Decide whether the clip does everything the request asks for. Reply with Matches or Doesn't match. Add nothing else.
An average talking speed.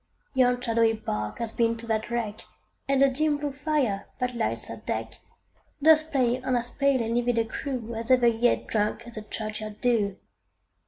Matches